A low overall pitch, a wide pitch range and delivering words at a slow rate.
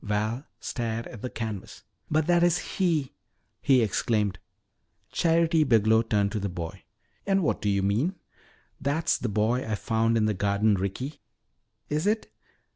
No: low, 115 Hz; wide, 6.6 semitones; average, 160 wpm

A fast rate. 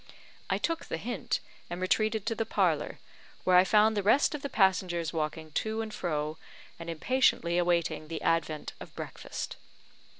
No: average, 165 wpm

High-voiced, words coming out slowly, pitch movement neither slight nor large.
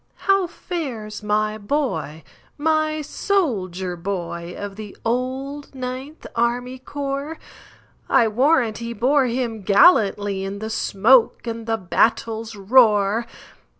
Yes: high, 230 Hz; slow, 95 wpm; average, 5.0 semitones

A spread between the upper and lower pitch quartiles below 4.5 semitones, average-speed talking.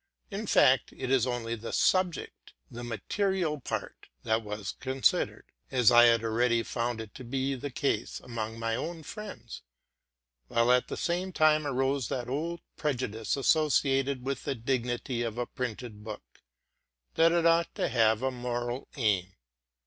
Yes: average, 3.5 semitones; average, 160 wpm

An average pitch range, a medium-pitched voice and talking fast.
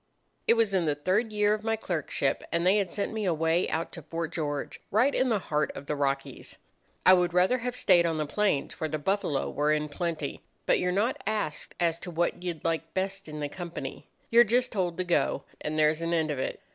Yes: average, 4.7 semitones; medium, 175 Hz; fast, 230 wpm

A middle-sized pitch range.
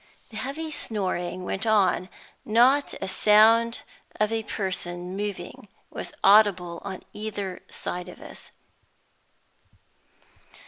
Yes: average, 3.1 semitones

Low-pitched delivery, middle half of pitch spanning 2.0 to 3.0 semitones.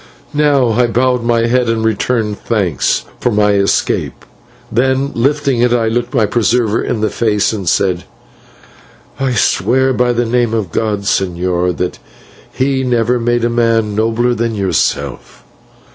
Yes: low, 115 Hz; average, 2.7 semitones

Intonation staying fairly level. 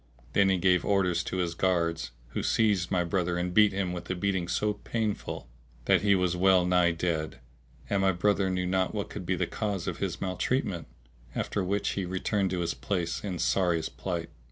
Yes: narrow, 1.9 semitones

